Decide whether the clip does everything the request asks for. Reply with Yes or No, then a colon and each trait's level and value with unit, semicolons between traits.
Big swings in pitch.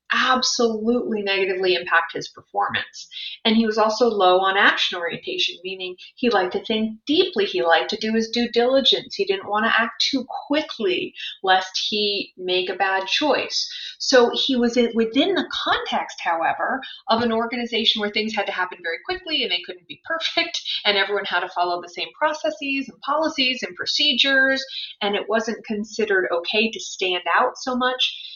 Yes: wide, 7.0 semitones